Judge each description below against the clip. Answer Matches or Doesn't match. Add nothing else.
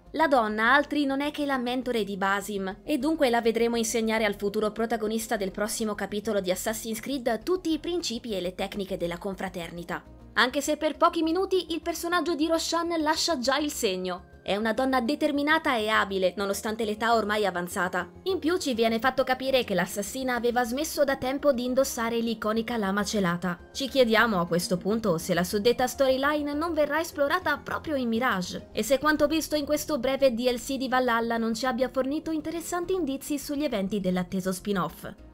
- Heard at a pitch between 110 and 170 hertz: Doesn't match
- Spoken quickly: Matches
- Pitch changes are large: Matches